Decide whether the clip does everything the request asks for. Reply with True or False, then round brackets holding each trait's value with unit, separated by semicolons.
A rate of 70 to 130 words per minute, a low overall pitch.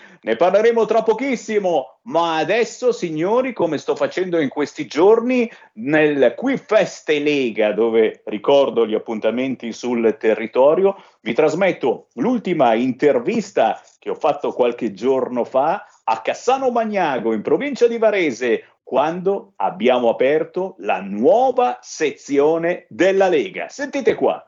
False (125 wpm; 185 Hz)